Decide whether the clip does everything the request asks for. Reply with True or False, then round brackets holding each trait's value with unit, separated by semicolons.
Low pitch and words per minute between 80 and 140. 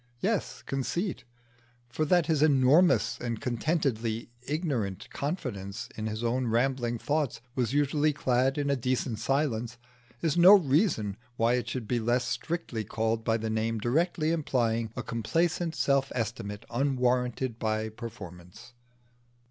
True (125 Hz; 135 wpm)